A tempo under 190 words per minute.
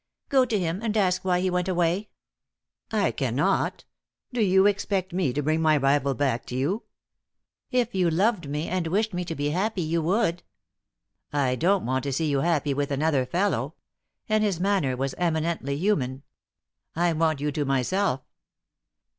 Yes: average, 170 wpm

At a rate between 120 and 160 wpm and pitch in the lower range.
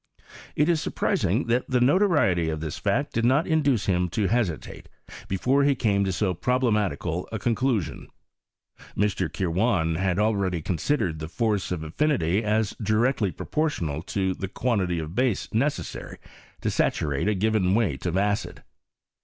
Yes: average, 155 wpm; low, 105 Hz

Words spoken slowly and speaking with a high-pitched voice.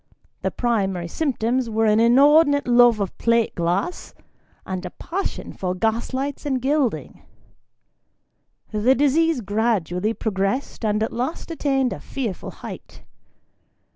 Yes: slow, 130 wpm; high, 235 Hz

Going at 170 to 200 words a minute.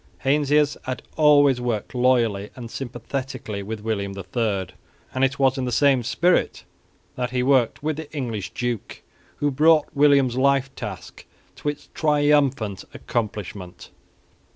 No: slow, 135 wpm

